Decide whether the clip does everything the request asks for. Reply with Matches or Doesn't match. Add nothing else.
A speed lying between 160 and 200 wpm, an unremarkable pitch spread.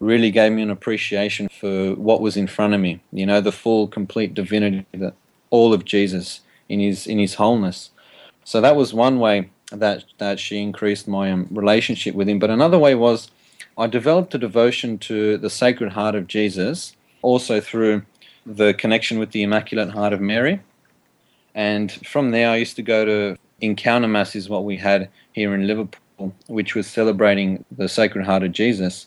Doesn't match